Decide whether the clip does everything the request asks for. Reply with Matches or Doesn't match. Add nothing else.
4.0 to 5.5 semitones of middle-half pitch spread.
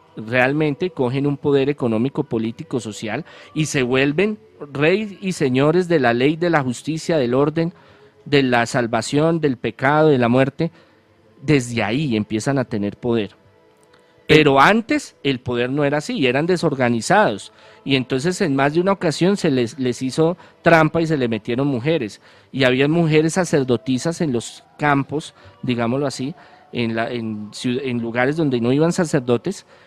Matches